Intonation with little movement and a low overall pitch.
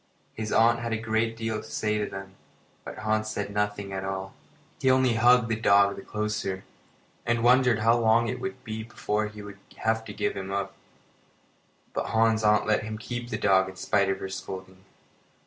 Yes: narrow, 2.2 semitones; low, 110 Hz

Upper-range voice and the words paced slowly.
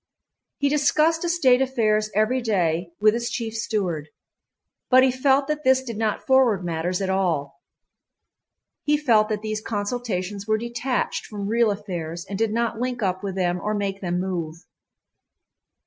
No: high, 215 Hz; average, 160 wpm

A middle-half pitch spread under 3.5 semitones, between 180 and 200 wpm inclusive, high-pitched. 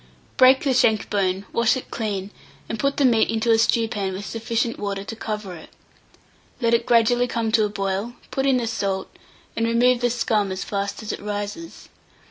Yes: average, 2.9 semitones; average, 195 wpm; high, 225 Hz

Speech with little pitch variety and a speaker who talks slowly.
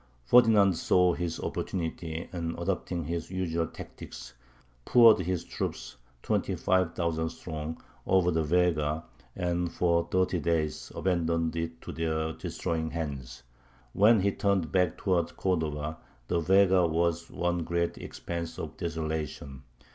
Yes: narrow, 2.1 semitones; slow, 130 wpm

